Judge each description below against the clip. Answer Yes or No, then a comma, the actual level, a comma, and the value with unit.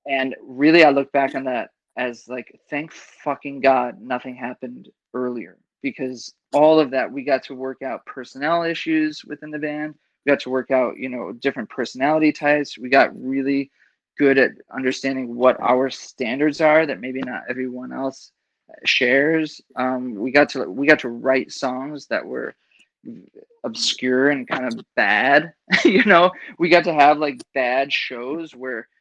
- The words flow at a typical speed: Yes, average, 170 wpm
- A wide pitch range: No, average, 2.8 semitones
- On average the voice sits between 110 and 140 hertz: Yes, low, 135 Hz